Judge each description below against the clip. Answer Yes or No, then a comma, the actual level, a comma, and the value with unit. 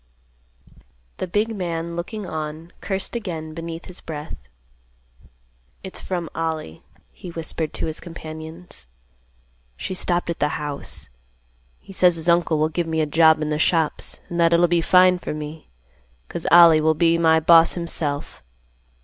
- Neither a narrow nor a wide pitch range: No, narrow, 1.8 semitones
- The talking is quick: No, average, 155 wpm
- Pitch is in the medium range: Yes, medium, 165 Hz